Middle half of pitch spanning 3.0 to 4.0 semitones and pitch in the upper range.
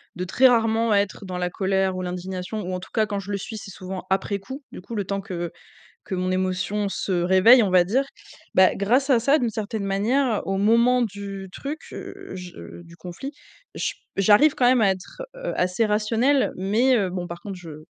Yes: average, 3.7 semitones; high, 200 Hz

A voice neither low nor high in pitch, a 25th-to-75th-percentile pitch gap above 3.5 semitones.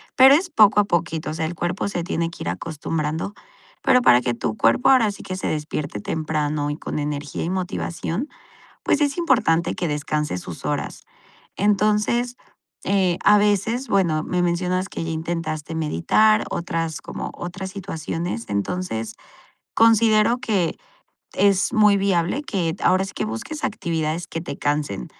Yes: medium, 175 Hz; average, 4.9 semitones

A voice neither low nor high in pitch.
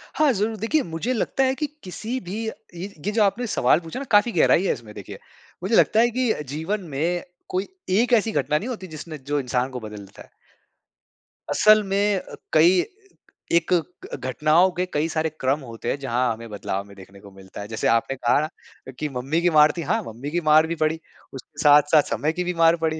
Yes: medium, 160 Hz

